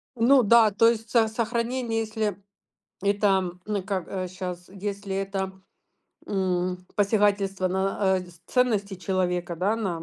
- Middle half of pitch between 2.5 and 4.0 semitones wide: Yes, average, 2.9 semitones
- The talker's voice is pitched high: Yes, high, 195 Hz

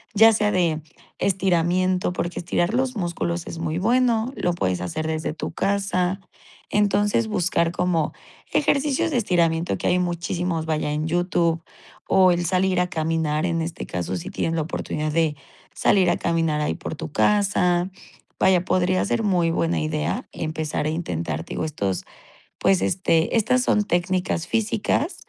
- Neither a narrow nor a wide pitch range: Yes, average, 3.0 semitones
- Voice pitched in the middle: Yes, medium, 175 Hz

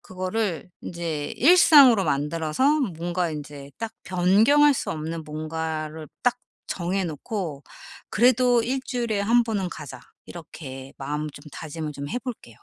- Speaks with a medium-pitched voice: Yes, medium, 175 Hz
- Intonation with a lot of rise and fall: Yes, wide, 7.0 semitones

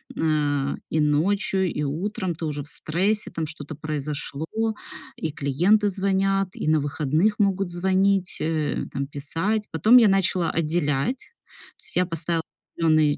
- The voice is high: No, medium, 165 Hz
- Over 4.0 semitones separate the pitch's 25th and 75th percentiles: Yes, average, 4.5 semitones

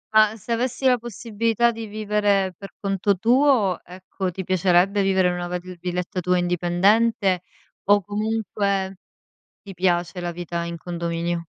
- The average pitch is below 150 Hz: No, high, 190 Hz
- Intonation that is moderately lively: Yes, average, 3.2 semitones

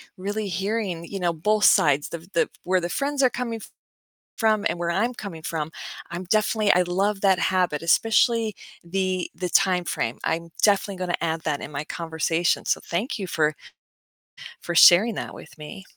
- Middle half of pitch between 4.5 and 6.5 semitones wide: No, average, 3.8 semitones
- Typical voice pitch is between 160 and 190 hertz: Yes, medium, 185 Hz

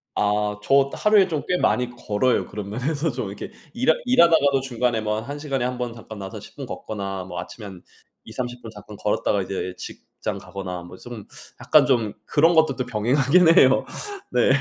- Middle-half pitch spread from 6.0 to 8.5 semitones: No, average, 5.2 semitones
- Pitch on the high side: No, low, 120 Hz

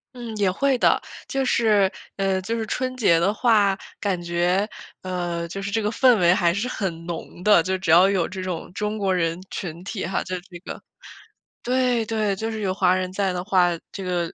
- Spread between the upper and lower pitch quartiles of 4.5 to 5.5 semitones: No, average, 3.2 semitones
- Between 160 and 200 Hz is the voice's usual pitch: Yes, high, 195 Hz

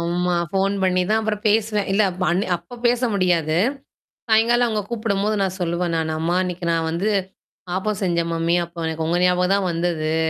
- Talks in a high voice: No, medium, 180 Hz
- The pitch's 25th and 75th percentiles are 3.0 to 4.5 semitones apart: Yes, average, 3.6 semitones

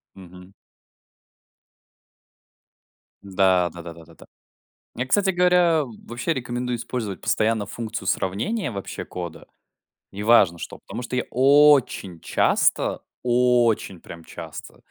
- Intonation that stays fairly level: No, average, 5.2 semitones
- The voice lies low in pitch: Yes, low, 115 Hz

